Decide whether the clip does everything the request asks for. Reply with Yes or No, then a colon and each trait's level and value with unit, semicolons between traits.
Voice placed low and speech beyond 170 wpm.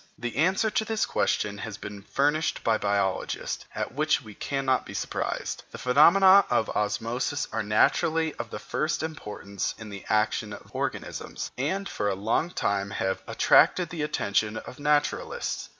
No: low, 125 Hz; average, 160 wpm